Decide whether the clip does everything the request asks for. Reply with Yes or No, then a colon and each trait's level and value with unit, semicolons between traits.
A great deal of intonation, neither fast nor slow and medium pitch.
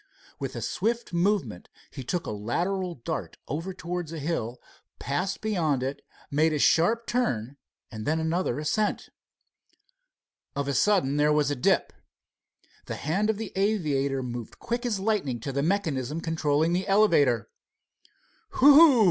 Yes: wide, 5.9 semitones; average, 150 wpm; medium, 160 Hz